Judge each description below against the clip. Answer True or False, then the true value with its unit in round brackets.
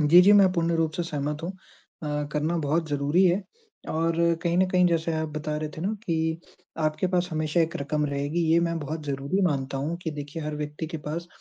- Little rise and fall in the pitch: True (2.3 semitones)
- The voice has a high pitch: False (160 Hz)